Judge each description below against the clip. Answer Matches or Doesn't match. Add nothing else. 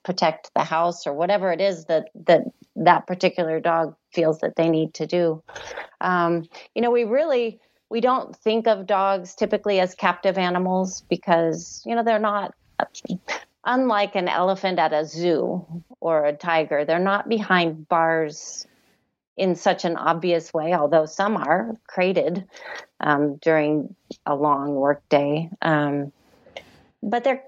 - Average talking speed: Matches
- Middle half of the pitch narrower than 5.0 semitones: Matches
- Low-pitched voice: Doesn't match